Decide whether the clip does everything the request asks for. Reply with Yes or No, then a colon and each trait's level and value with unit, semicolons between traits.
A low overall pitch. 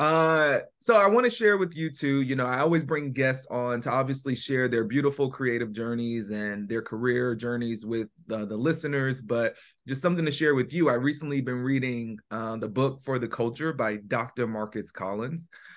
Yes: low, 130 Hz